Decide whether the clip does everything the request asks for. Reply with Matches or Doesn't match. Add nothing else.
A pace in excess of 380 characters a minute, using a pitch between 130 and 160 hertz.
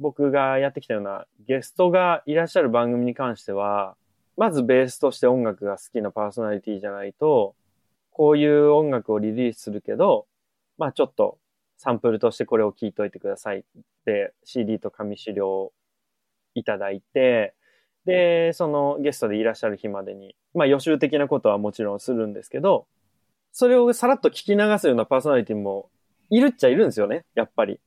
Matches